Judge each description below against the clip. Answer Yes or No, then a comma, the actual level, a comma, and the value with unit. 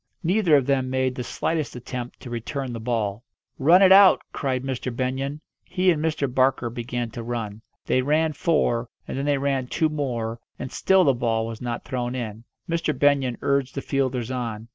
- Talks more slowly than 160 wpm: No, average, 190 wpm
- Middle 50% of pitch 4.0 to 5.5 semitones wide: No, average, 3.3 semitones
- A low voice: Yes, low, 130 Hz